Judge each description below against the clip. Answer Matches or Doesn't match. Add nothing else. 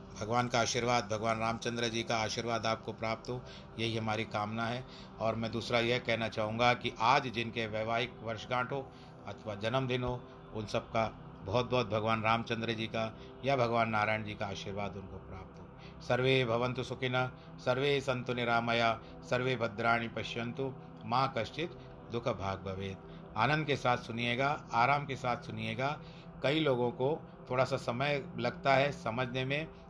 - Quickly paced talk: Doesn't match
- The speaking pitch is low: Matches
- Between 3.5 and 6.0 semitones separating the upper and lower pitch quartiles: Doesn't match